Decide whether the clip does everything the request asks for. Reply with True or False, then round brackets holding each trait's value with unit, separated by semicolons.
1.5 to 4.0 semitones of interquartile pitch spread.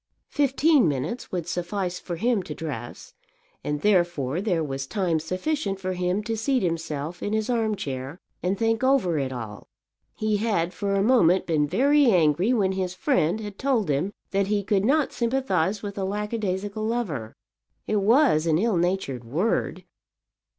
False (5.1 semitones)